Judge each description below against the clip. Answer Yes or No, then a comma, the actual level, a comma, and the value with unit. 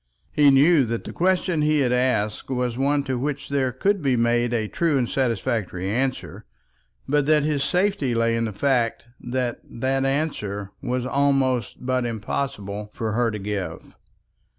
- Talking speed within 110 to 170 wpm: Yes, average, 165 wpm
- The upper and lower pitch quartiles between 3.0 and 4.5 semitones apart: Yes, average, 3.5 semitones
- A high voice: No, low, 130 Hz